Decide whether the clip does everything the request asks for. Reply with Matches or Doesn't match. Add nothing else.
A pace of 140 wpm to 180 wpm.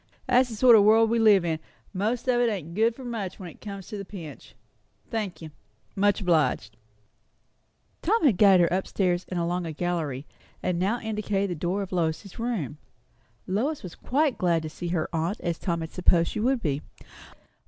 Doesn't match